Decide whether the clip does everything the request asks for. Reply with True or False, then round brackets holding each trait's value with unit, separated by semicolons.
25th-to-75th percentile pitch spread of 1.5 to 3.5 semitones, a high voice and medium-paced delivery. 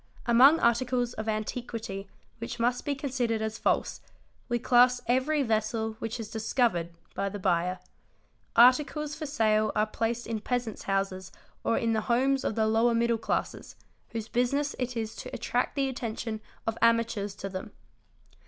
True (2.4 semitones; 230 Hz; 160 wpm)